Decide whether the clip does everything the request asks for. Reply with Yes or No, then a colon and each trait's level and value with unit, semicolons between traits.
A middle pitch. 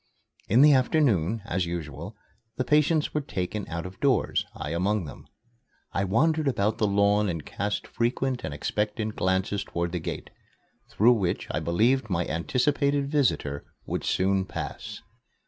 No: low, 105 Hz